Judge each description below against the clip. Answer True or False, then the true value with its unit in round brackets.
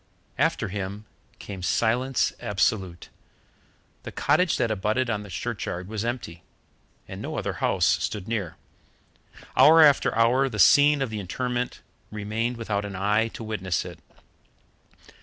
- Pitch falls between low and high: False (110 Hz)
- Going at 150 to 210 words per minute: False (140 wpm)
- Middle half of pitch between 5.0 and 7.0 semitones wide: False (3.8 semitones)